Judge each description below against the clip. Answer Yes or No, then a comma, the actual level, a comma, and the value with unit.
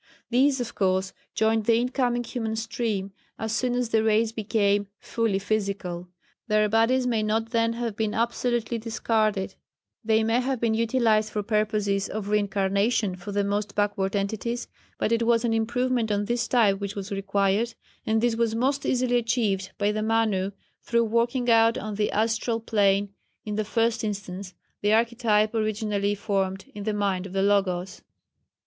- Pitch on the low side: No, high, 220 Hz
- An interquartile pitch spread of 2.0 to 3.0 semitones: Yes, narrow, 2.4 semitones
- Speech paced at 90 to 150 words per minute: No, average, 170 wpm